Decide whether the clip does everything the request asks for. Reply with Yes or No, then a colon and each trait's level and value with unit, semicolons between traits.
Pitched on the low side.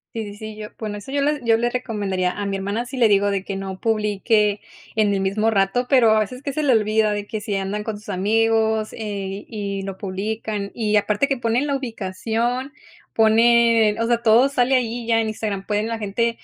No: high, 220 Hz